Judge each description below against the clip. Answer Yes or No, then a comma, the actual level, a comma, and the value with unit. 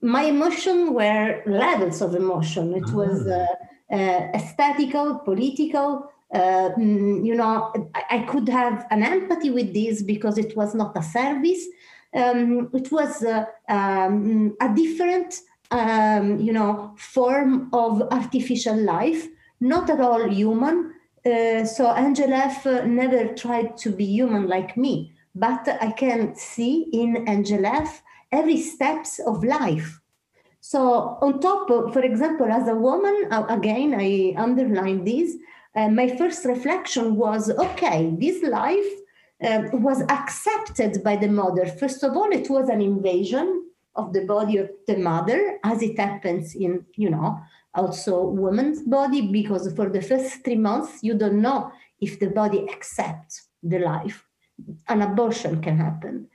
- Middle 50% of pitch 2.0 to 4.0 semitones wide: No, average, 5.3 semitones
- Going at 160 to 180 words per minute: No, average, 145 wpm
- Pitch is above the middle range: Yes, high, 230 Hz